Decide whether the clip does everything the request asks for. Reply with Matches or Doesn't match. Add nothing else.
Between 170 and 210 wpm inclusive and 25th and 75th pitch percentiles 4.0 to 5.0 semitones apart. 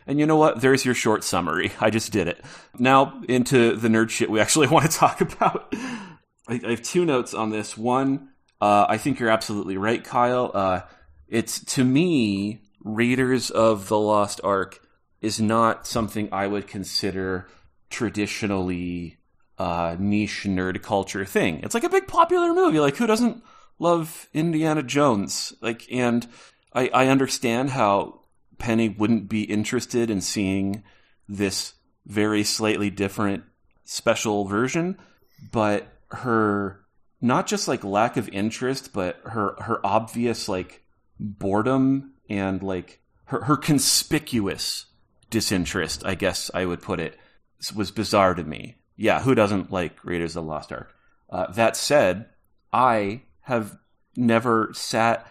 Doesn't match